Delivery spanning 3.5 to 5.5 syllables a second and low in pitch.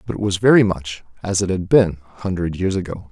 No: 6.0 syllables/s; very low, 95 Hz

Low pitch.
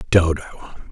Yes: very low, 80 Hz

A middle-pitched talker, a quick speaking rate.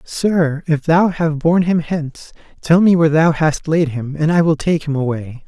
Yes: medium, 155 Hz; fast, 220 wpm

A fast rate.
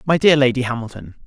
No: average, 190 wpm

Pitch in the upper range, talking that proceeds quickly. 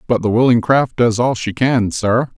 No: low, 115 Hz; fast, 225 wpm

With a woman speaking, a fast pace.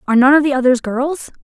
Yes: female; fast, 250 wpm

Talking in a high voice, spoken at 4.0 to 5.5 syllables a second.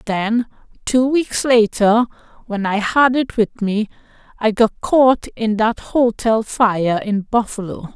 No: high, 225 Hz; 3.6 syllables/s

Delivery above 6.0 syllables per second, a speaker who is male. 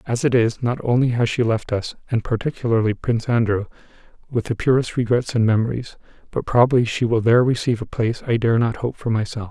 Yes: 6.2 syllables/s; male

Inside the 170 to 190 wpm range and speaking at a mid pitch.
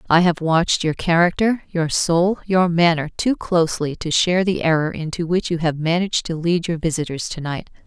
No: average, 200 wpm; medium, 170 Hz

